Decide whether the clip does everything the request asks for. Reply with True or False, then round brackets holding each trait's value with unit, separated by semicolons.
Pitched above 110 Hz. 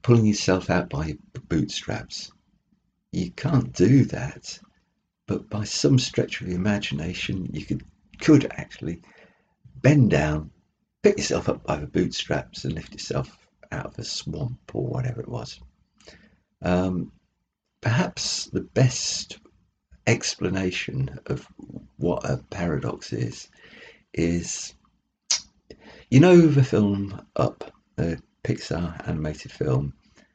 False (105 Hz)